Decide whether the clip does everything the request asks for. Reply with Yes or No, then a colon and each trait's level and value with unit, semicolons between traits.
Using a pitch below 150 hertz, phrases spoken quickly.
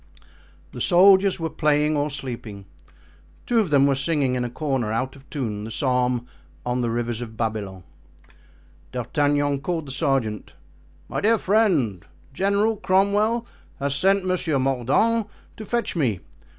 No: medium, 140 Hz; average, 145 wpm